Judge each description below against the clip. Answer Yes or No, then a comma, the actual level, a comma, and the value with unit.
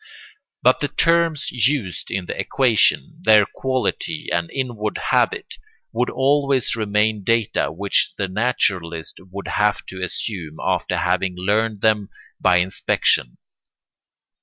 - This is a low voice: Yes, low, 105 Hz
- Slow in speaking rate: Yes, slow, 120 wpm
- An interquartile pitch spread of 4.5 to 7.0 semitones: Yes, average, 5.1 semitones